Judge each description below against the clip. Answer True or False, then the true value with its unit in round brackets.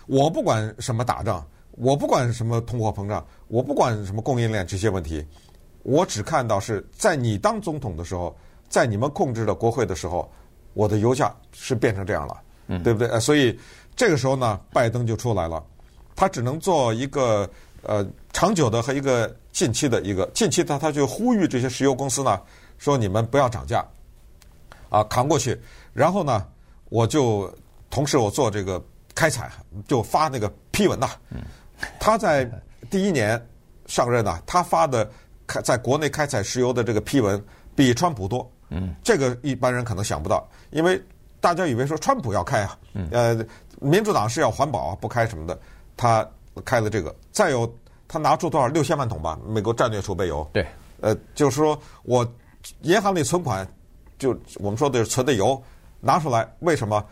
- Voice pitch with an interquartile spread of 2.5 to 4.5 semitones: False (5.3 semitones)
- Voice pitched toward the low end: True (115 Hz)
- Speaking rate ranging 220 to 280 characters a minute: True (270 characters per minute)